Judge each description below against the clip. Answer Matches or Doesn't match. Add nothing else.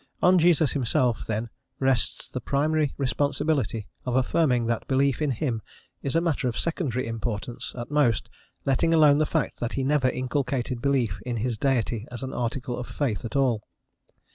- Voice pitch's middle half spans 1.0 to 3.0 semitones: Doesn't match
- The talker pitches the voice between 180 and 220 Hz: Doesn't match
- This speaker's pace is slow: Doesn't match